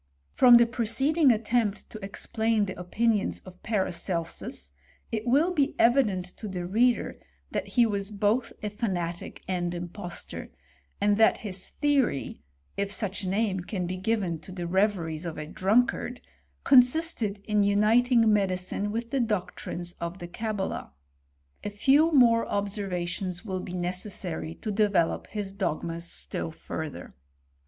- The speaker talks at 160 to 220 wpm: No, average, 145 wpm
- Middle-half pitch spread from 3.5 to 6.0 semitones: Yes, average, 4.1 semitones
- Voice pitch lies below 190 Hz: No, high, 205 Hz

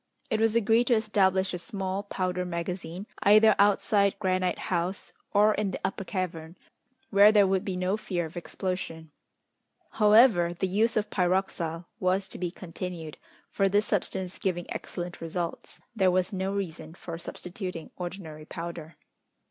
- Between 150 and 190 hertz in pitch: Yes, medium, 185 Hz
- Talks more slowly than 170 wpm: Yes, average, 150 wpm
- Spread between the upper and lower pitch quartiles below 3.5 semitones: Yes, narrow, 2.5 semitones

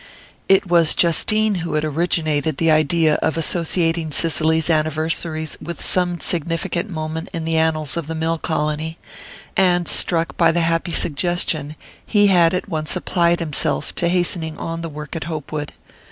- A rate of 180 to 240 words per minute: No, average, 155 wpm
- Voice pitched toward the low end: No, medium, 165 Hz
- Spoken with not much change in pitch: Yes, narrow, 1.7 semitones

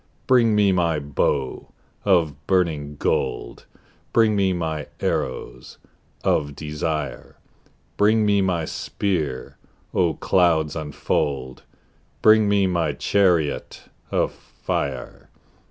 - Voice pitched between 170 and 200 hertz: No, very low, 85 Hz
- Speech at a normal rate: No, slow, 100 wpm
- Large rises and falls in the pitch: No, average, 5.0 semitones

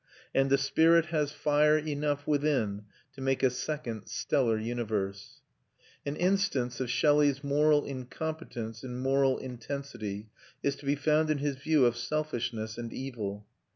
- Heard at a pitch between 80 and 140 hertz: Yes, low, 135 Hz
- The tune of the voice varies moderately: Yes, average, 3.8 semitones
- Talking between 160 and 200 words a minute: No, average, 145 wpm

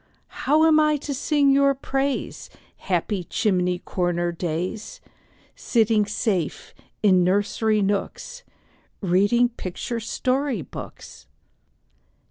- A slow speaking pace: Yes, slow, 100 wpm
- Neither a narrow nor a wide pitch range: No, wide, 6.9 semitones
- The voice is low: No, high, 215 Hz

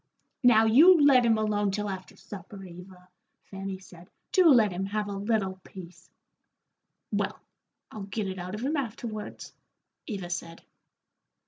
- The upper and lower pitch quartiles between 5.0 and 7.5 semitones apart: No, average, 3.0 semitones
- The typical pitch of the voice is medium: No, high, 205 Hz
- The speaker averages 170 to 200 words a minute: No, average, 145 wpm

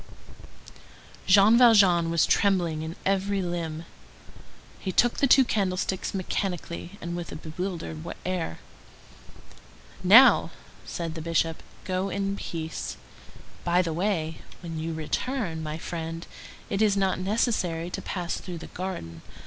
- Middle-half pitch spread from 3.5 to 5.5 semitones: No, average, 3.1 semitones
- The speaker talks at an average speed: No, slow, 130 wpm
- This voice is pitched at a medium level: Yes, medium, 180 Hz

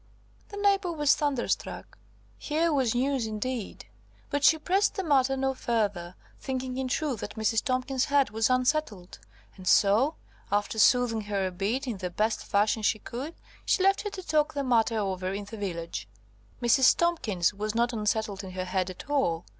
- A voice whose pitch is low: No, high, 235 Hz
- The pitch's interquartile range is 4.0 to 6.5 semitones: Yes, wide, 5.6 semitones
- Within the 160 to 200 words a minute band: Yes, average, 180 wpm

